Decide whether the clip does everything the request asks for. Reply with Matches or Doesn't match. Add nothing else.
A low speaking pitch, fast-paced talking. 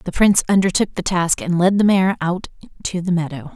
Doesn't match